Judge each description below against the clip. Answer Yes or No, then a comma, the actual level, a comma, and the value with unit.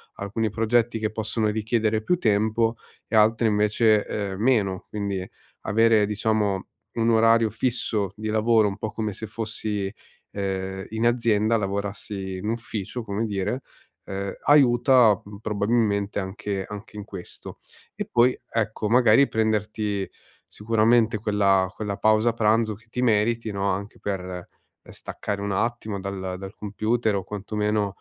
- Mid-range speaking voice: No, low, 105 Hz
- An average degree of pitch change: No, narrow, 2.1 semitones